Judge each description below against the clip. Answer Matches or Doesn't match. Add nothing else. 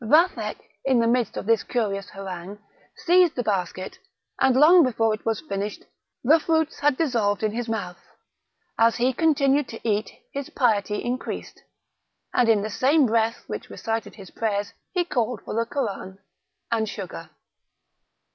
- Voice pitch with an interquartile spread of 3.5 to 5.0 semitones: Matches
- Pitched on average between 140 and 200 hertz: Doesn't match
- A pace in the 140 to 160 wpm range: Matches